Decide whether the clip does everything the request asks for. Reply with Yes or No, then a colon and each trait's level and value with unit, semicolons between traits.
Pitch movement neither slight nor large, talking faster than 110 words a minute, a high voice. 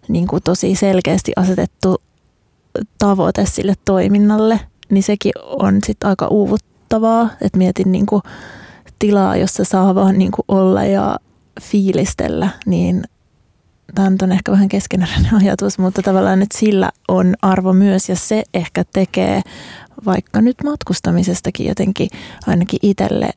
No: narrow, 1.6 semitones; average, 130 wpm; high, 195 Hz